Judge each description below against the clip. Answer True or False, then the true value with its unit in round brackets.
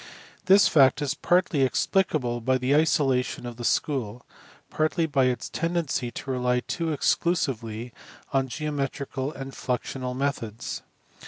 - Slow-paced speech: True (130 wpm)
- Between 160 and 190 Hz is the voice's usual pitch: False (135 Hz)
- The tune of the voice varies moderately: True (3.6 semitones)